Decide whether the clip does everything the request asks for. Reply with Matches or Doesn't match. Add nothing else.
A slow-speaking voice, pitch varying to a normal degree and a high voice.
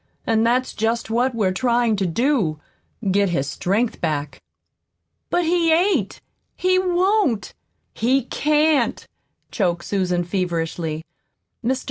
Doesn't match